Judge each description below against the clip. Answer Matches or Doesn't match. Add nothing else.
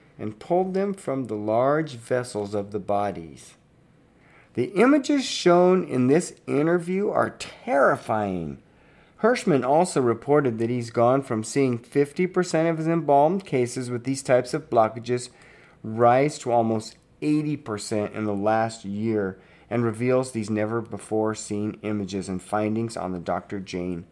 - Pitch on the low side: Matches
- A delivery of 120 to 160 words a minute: Matches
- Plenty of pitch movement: Matches